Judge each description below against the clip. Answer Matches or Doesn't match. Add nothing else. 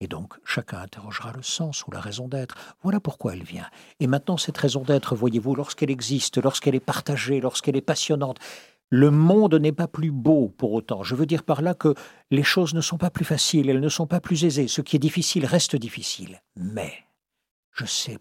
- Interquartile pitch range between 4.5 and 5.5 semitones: Doesn't match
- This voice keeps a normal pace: Matches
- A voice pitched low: Doesn't match